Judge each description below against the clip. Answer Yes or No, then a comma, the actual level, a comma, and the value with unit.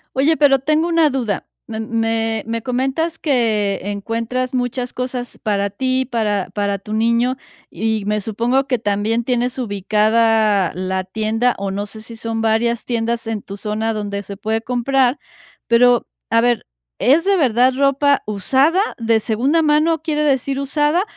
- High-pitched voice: Yes, high, 230 Hz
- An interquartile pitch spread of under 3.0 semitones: No, average, 3.5 semitones